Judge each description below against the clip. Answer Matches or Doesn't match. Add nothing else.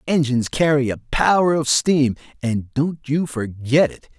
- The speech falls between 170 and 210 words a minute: Doesn't match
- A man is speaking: Matches